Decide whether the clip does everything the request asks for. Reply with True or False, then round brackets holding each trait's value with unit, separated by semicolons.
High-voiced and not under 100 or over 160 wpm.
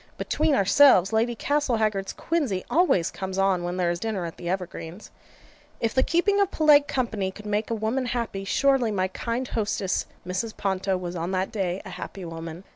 False (205 Hz; 185 wpm)